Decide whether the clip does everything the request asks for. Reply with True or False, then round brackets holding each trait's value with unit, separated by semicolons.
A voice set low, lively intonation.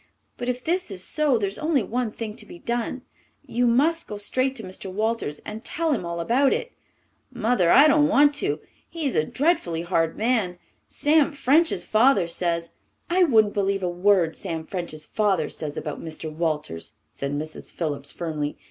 False (210 Hz; 8.1 semitones)